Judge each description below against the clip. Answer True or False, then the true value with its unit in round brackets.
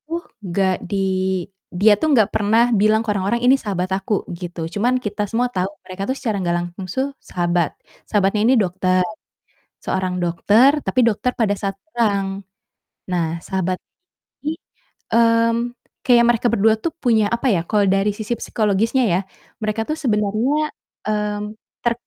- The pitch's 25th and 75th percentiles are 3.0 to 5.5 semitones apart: True (3.6 semitones)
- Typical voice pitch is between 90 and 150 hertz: False (210 Hz)